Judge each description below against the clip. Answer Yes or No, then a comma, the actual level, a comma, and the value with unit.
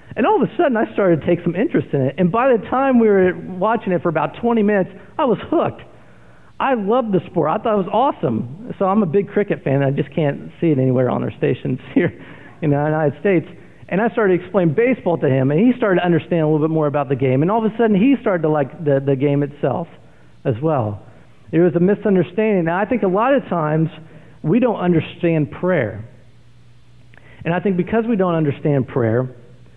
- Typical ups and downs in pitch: No, wide, 6.2 semitones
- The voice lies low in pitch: No, medium, 175 Hz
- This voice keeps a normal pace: No, fast, 235 wpm